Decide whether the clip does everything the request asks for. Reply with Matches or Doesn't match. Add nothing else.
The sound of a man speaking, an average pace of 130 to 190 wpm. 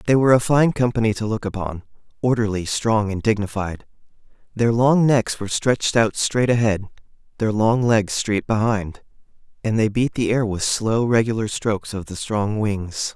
Matches